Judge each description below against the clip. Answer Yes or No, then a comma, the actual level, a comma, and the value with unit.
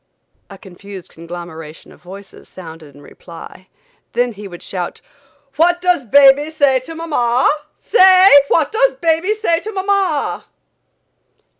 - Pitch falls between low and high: No, very high, 270 Hz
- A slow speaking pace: Yes, slow, 130 wpm